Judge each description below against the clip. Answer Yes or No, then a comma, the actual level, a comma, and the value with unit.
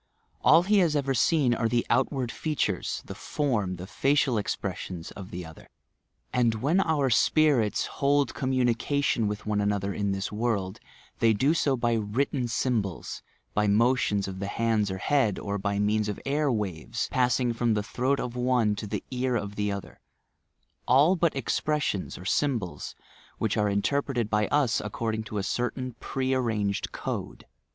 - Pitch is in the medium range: No, low, 115 Hz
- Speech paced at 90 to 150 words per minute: No, average, 170 wpm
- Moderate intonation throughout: Yes, average, 4.5 semitones